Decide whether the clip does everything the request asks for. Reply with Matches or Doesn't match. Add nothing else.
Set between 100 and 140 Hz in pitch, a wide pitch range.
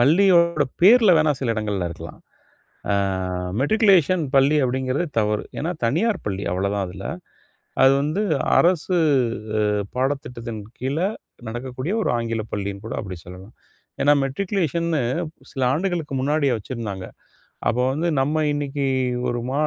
Matches